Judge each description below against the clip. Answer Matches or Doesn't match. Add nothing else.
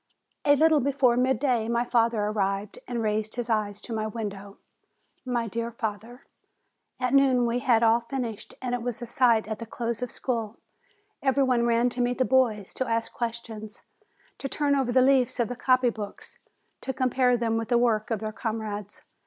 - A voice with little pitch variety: Matches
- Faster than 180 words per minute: Matches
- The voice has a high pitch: Matches